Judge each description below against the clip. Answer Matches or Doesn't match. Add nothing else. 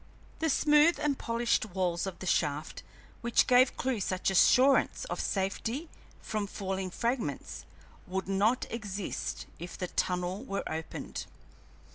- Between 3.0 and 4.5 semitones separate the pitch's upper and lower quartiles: Doesn't match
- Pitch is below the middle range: Doesn't match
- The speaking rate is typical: Doesn't match